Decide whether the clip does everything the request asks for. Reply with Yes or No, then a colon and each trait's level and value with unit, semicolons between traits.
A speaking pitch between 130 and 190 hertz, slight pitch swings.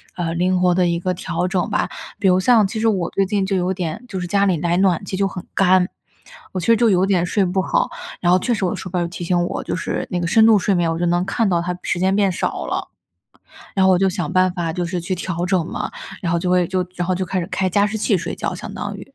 Yes: medium, 185 Hz; narrow, 1.8 semitones